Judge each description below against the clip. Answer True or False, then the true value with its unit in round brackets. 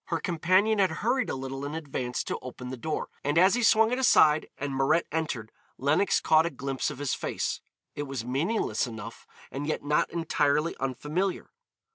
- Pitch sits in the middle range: True (150 Hz)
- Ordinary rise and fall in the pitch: True (4.3 semitones)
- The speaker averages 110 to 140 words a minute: False (185 wpm)